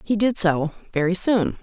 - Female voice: Yes, female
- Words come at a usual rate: Yes, average, 185 wpm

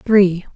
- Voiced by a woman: Yes, female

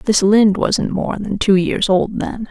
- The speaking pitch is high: Yes, high, 200 Hz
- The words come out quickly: Yes, fast, 215 wpm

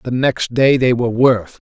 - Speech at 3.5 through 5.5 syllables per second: Yes, 5.4 syllables/s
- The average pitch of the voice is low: Yes, low, 125 Hz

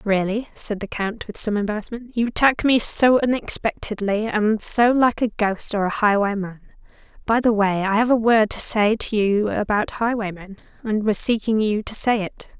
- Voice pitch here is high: Yes, high, 215 Hz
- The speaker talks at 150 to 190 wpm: Yes, average, 185 wpm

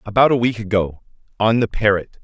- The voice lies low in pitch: Yes, low, 105 Hz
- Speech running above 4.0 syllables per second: Yes, 5.7 syllables/s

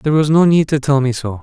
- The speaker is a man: Yes, male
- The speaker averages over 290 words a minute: Yes, fast, 335 wpm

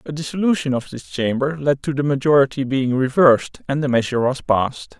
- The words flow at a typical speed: Yes, average, 190 wpm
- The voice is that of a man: Yes, male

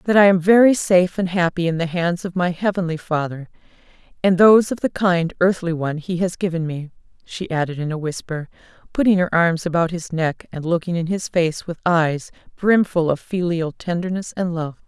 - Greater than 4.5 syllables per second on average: Yes, 5.3 syllables/s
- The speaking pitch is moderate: Yes, medium, 175 Hz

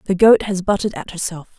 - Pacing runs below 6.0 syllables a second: Yes, 5.7 syllables/s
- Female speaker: Yes, female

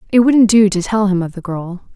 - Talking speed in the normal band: No, fast, 275 wpm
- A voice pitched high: Yes, high, 200 Hz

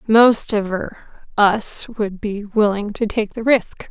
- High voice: Yes, high, 210 Hz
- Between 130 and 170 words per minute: Yes, average, 140 wpm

